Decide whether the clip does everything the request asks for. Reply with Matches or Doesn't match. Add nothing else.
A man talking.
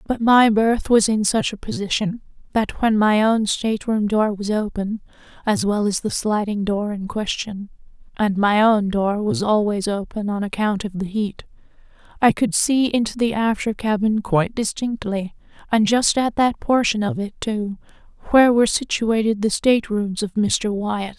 Doesn't match